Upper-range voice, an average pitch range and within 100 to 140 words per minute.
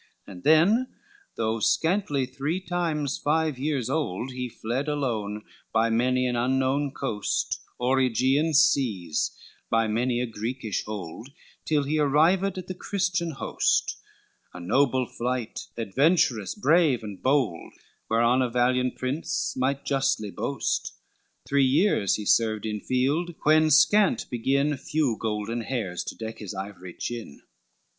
No: low, 130 Hz; average, 4.9 semitones; slow, 135 wpm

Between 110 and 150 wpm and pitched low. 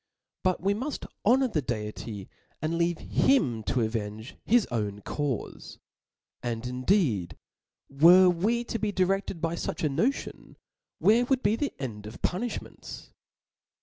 No: average, 140 wpm; medium, 165 Hz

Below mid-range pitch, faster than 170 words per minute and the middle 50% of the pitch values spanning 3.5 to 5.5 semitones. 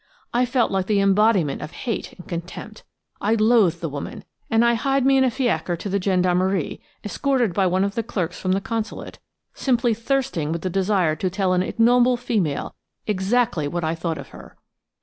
No: high, 200 Hz; average, 190 wpm; average, 4.8 semitones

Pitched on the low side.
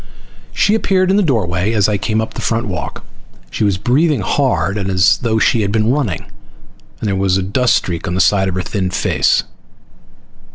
Yes: low, 105 Hz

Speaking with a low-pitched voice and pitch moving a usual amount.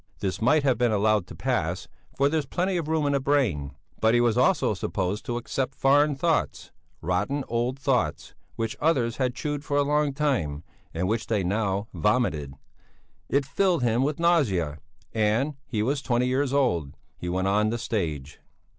No: low, 120 Hz; wide, 6.2 semitones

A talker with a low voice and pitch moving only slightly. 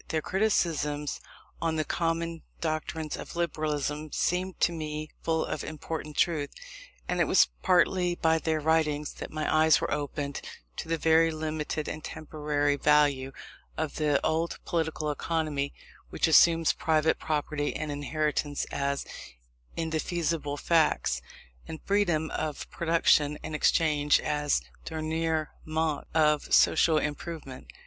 No: medium, 155 Hz; narrow, 1.6 semitones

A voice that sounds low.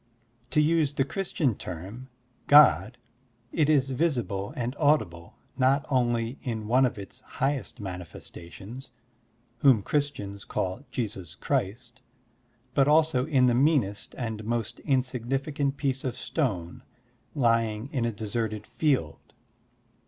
Yes: low, 125 Hz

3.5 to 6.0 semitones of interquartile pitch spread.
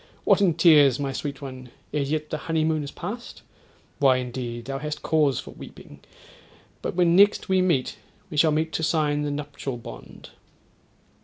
No: average, 3.0 semitones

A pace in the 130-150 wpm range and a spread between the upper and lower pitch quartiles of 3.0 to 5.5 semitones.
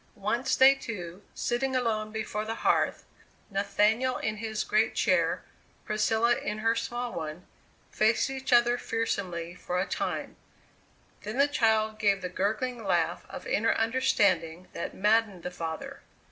Yes: average, 145 wpm; average, 3.3 semitones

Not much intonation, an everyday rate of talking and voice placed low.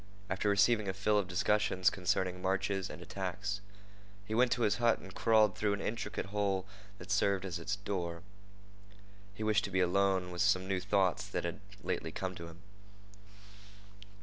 Yes: narrow, 2.0 semitones; average, 175 wpm; low, 100 Hz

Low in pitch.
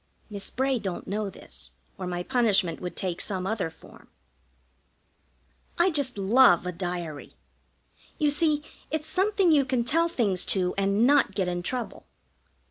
No: high, 210 Hz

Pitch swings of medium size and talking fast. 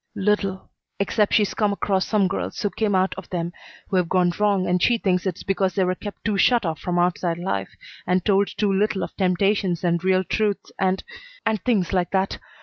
No: narrow, 2.1 semitones; fast, 210 wpm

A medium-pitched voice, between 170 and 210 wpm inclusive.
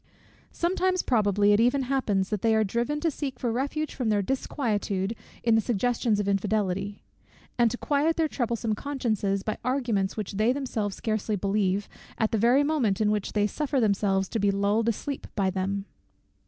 No: high, 220 Hz; average, 180 wpm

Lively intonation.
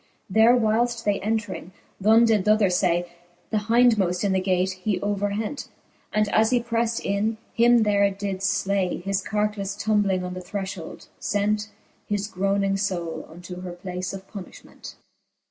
No: narrow, 2.5 semitones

